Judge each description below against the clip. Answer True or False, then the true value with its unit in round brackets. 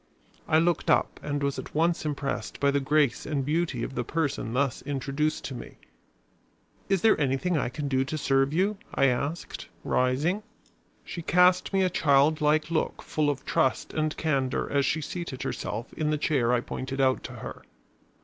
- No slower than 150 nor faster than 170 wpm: False (185 wpm)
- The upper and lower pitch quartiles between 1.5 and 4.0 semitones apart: True (2.9 semitones)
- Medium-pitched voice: True (145 Hz)